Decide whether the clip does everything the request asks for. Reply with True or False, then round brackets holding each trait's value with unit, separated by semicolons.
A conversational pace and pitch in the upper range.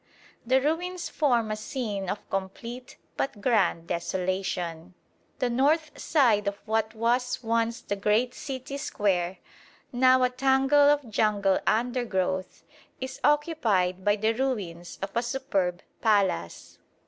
False (125 wpm; 225 Hz)